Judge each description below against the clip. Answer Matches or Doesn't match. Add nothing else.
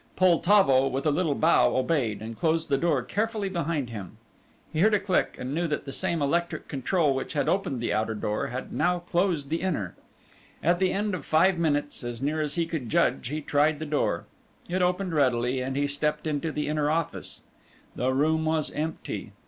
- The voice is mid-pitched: Matches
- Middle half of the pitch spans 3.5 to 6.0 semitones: Matches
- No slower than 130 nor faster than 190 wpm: Doesn't match